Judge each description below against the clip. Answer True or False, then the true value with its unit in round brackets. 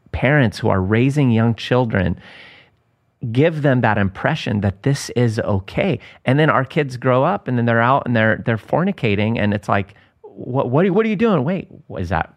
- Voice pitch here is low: True (120 Hz)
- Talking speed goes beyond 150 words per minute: True (205 wpm)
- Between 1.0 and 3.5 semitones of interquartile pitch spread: False (4.5 semitones)